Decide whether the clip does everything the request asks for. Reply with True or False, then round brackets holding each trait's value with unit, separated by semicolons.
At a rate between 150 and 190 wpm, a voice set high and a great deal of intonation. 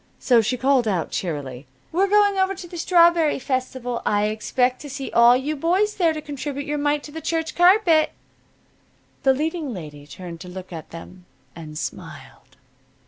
True (175 wpm; 270 Hz; 8.1 semitones)